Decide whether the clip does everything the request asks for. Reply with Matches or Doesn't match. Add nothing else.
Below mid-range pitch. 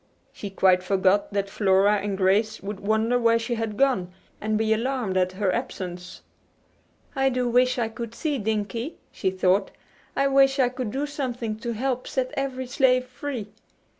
Doesn't match